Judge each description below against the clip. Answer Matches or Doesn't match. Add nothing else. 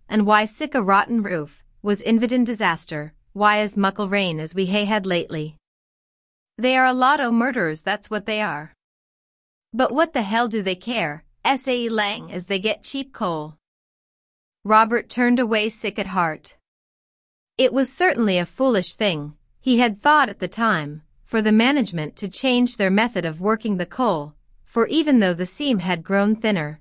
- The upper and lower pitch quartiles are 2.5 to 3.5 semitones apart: Doesn't match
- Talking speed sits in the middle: Matches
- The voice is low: Doesn't match